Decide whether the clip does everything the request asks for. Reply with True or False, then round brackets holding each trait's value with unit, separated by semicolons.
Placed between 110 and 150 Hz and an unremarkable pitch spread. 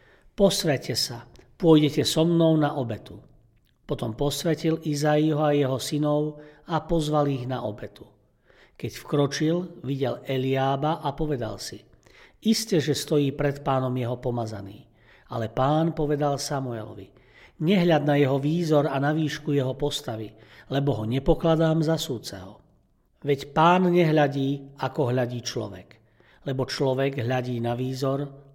True (140 Hz; 3.6 semitones)